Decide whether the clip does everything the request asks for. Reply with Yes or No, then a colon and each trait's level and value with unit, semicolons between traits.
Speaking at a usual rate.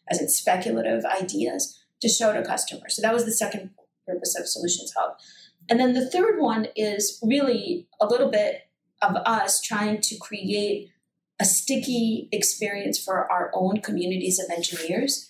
Yes: average, 160 wpm